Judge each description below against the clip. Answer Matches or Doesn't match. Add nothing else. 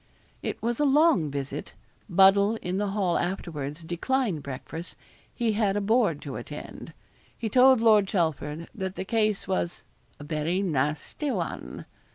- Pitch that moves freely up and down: Matches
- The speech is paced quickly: Doesn't match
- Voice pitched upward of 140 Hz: Matches